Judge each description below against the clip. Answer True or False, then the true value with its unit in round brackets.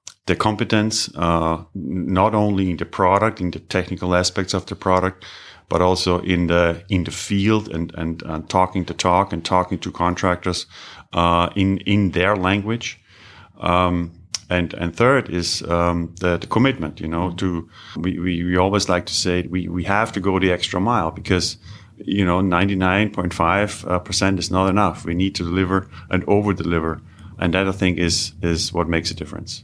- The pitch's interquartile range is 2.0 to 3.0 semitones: True (2.5 semitones)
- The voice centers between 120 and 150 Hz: False (90 Hz)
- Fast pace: False (185 wpm)